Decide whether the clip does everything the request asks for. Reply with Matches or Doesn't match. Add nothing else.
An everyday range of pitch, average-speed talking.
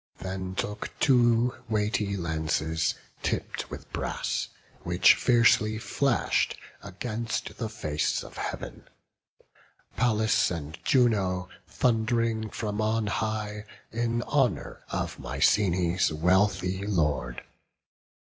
Doesn't match